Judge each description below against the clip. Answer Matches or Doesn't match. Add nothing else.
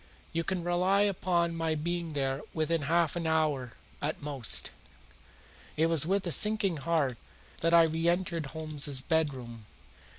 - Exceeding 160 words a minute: Doesn't match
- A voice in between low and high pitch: Matches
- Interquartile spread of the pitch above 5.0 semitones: Doesn't match